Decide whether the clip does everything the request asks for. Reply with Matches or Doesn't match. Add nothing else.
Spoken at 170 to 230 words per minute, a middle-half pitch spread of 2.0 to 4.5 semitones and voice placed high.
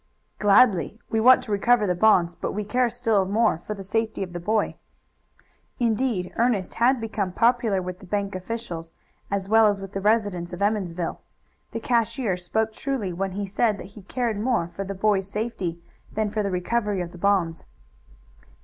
Matches